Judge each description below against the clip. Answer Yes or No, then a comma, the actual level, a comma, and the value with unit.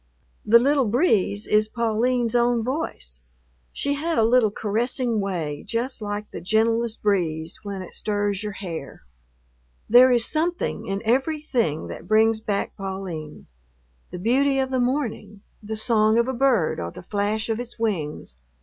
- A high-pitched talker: Yes, high, 220 Hz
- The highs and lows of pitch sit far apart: No, average, 3.5 semitones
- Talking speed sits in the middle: Yes, average, 155 wpm